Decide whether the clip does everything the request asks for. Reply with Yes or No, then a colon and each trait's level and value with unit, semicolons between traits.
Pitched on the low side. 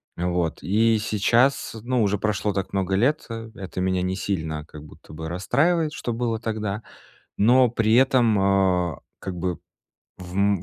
Yes: low, 105 Hz